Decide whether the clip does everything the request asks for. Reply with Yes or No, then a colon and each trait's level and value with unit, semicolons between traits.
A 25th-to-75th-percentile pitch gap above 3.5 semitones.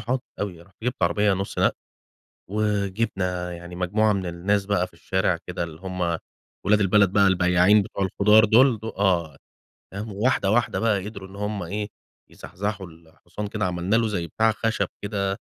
No: average, 2.8 semitones